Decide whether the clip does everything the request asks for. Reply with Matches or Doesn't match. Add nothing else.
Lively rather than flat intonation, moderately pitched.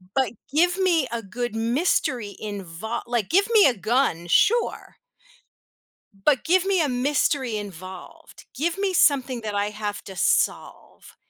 Doesn't match